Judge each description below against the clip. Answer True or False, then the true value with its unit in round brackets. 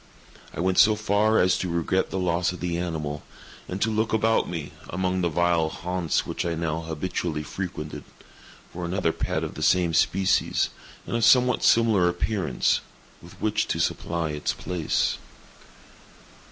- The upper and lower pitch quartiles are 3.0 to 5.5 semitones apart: False (2.5 semitones)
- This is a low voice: True (90 Hz)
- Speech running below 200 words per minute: True (160 wpm)